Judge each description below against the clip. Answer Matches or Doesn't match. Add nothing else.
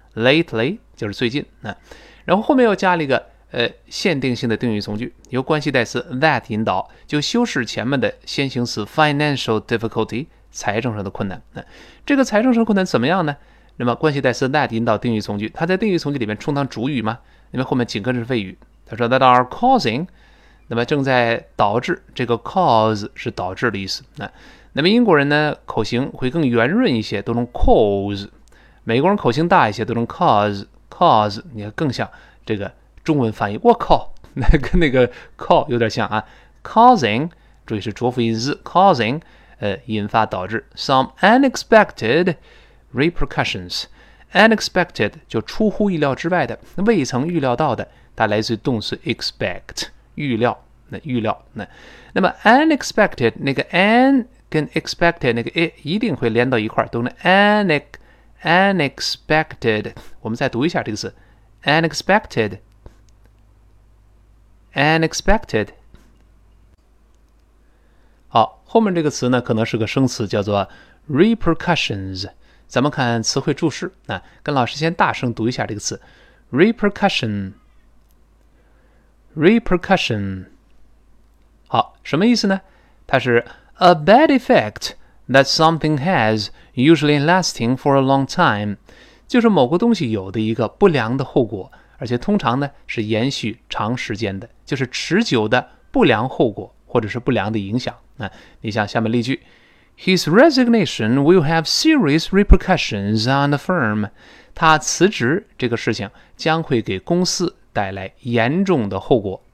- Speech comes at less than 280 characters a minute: Doesn't match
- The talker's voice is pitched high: Doesn't match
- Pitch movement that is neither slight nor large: Doesn't match